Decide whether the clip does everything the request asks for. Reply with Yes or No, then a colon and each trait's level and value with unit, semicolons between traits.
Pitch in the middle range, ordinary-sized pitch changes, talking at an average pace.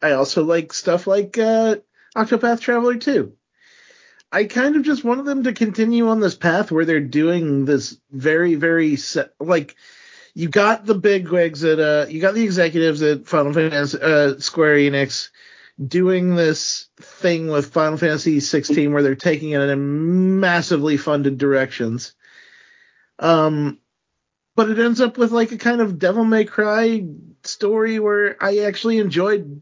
No: medium, 175 Hz; wide, 6.6 semitones; average, 160 wpm